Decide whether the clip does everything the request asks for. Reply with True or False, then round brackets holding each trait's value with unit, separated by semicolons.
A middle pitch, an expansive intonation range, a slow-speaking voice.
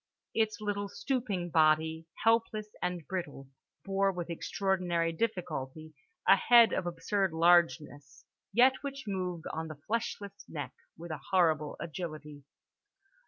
False (175 Hz; 4.3 semitones; 120 wpm)